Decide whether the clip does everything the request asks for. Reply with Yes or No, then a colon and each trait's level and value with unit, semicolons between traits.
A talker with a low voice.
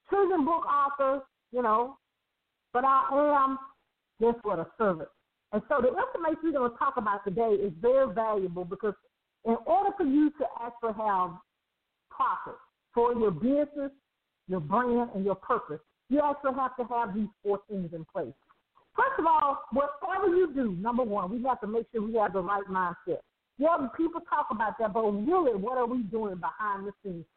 No: high, 245 Hz